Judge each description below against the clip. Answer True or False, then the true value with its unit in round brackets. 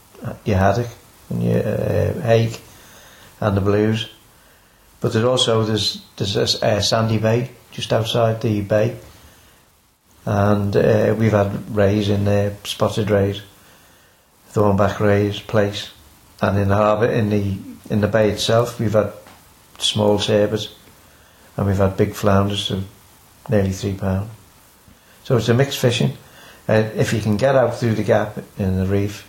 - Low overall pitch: True (105 Hz)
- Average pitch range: False (1.9 semitones)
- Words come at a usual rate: True (150 wpm)